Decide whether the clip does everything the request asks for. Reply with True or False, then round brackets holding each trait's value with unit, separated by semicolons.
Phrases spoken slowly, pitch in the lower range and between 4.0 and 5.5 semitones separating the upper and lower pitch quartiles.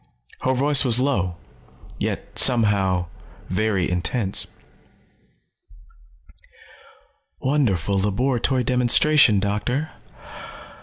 True (65 wpm; 115 Hz; 5.2 semitones)